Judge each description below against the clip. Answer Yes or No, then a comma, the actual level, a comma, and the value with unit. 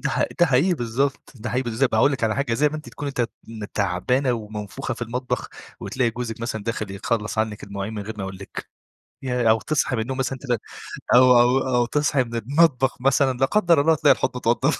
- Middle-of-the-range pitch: No, low, 125 Hz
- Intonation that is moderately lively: Yes, average, 3.4 semitones